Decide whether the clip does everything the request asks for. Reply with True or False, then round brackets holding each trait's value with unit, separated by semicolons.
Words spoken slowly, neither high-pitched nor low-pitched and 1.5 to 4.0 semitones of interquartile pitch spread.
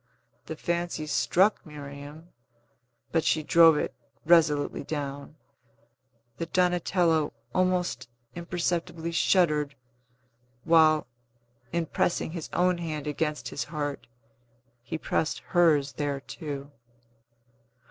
True (95 wpm; 160 Hz; 2.6 semitones)